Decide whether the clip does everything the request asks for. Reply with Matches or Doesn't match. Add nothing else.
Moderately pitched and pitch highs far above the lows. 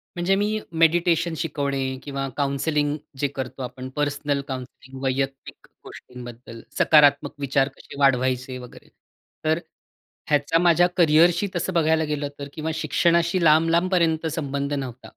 Doesn't match